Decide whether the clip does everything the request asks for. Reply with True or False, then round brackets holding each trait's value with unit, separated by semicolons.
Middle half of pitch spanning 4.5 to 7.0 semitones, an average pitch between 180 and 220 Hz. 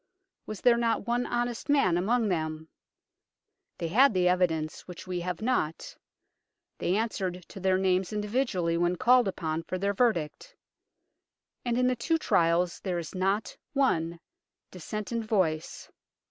True (5.3 semitones; 190 Hz)